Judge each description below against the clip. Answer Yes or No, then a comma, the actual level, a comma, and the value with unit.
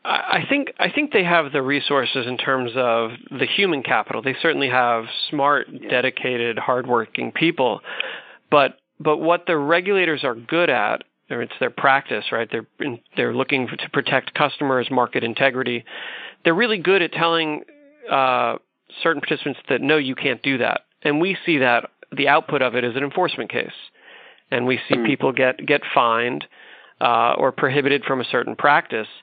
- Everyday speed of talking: Yes, average, 170 wpm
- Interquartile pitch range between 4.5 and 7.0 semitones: Yes, average, 4.8 semitones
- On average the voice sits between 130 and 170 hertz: Yes, medium, 140 Hz